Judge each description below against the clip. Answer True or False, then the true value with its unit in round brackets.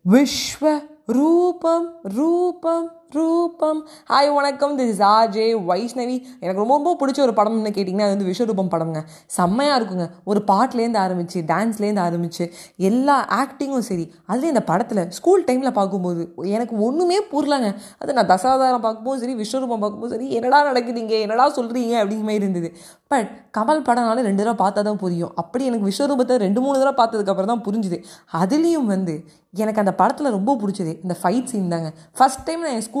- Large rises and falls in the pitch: True (6.0 semitones)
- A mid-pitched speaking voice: False (225 Hz)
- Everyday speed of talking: False (155 wpm)